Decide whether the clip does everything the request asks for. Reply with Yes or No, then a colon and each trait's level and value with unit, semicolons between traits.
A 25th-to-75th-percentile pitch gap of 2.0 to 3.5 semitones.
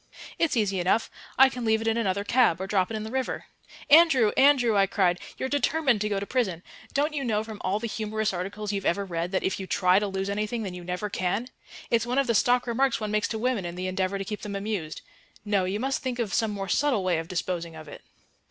No: average, 4.1 semitones